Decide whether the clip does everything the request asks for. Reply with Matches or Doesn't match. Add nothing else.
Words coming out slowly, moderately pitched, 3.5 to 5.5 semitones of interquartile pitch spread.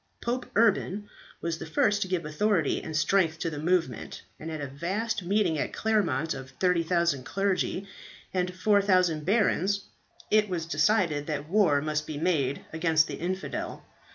Doesn't match